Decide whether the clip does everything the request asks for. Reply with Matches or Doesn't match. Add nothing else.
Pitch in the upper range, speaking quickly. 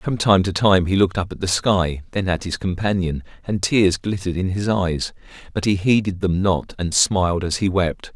Doesn't match